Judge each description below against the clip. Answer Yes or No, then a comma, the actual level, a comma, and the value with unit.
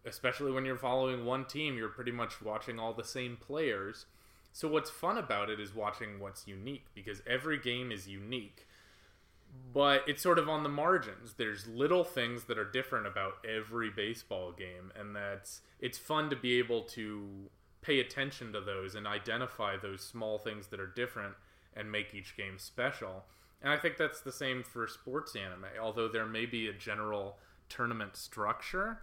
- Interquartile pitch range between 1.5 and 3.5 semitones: No, average, 4.1 semitones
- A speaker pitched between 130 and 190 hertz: No, low, 110 Hz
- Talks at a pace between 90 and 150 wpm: No, average, 180 wpm